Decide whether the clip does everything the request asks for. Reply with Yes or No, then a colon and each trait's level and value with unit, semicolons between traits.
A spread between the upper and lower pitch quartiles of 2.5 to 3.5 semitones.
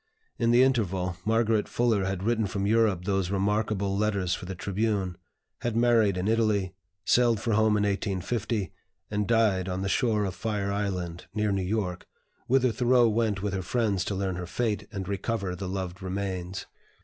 Yes: average, 2.9 semitones